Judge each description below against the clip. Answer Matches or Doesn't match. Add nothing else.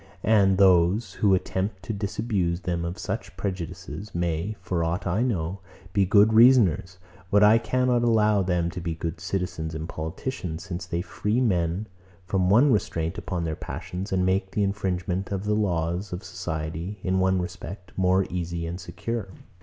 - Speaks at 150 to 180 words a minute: Matches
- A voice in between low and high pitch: Doesn't match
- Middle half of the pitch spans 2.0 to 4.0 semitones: Matches